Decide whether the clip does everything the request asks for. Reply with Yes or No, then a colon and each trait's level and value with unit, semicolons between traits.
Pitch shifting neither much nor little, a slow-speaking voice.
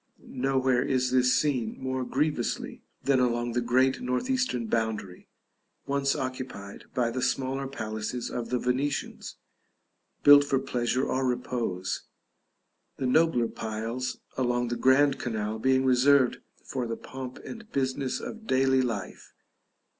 No: narrow, 2.0 semitones; slow, 130 wpm